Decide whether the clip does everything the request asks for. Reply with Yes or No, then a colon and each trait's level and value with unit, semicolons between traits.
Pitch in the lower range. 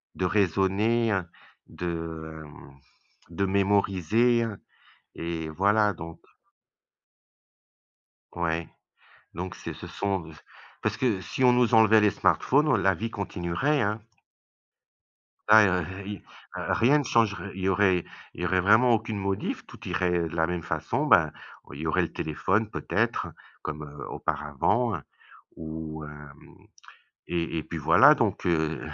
Yes: very low, 95 Hz